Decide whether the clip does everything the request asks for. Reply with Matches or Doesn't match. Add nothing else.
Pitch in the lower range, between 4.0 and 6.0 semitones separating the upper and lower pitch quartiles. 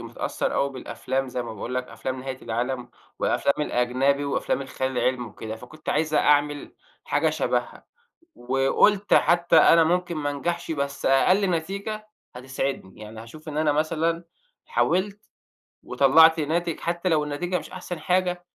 Doesn't match